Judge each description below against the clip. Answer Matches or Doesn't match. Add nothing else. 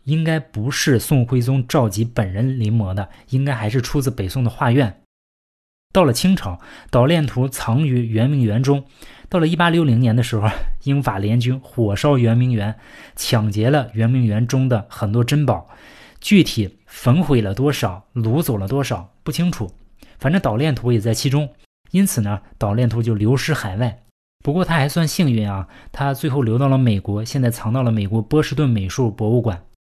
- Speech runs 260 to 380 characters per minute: Matches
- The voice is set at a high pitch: Doesn't match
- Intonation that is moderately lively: Matches